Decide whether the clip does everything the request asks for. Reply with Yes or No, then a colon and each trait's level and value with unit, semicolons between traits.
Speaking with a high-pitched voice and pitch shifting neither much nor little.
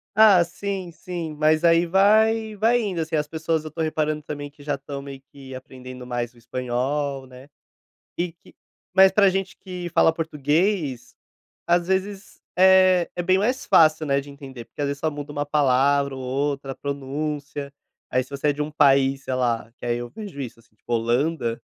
No: medium, 145 Hz; average, 4.5 semitones